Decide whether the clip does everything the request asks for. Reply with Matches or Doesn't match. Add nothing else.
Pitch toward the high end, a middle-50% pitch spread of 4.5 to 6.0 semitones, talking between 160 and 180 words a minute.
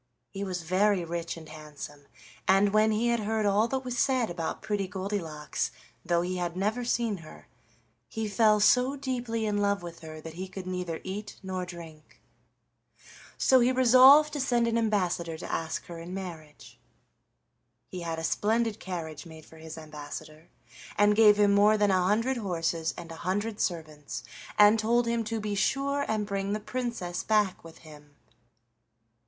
Matches